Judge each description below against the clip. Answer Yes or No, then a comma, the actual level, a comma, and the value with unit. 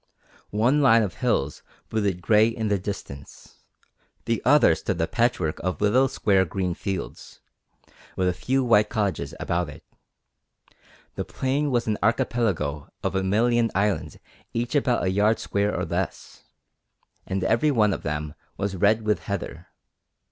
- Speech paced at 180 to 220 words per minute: No, average, 150 wpm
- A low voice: Yes, low, 105 Hz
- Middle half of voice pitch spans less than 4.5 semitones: Yes, average, 3.9 semitones